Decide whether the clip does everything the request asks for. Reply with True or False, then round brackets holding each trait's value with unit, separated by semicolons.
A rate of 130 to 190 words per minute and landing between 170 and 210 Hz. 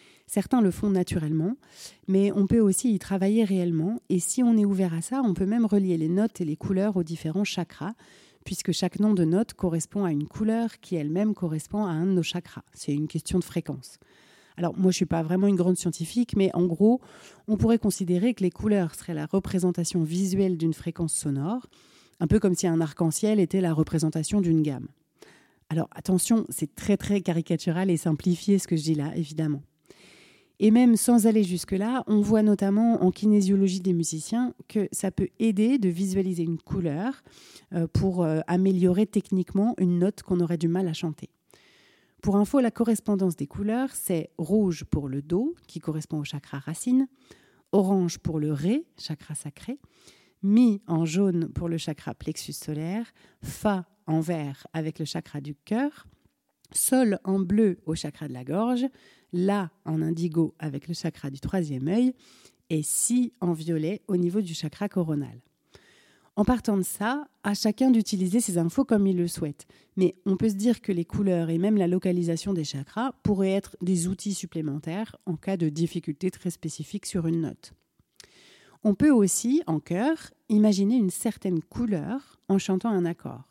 True (180 wpm; 185 Hz)